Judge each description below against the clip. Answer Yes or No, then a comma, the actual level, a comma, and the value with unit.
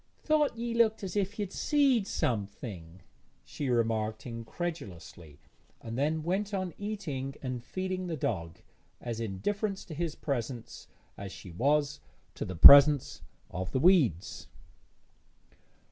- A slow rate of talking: Yes, slow, 130 wpm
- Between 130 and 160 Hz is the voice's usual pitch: Yes, medium, 140 Hz